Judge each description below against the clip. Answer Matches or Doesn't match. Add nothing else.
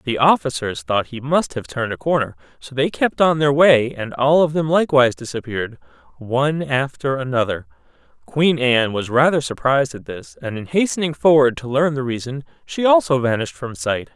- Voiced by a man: Matches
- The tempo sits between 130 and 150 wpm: Doesn't match